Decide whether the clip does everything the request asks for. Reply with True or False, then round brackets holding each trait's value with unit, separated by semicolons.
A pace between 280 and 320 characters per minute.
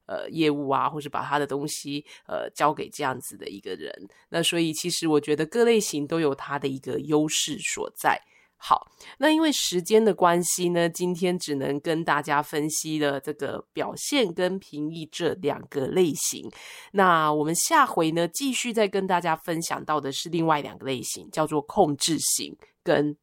False (265 characters per minute)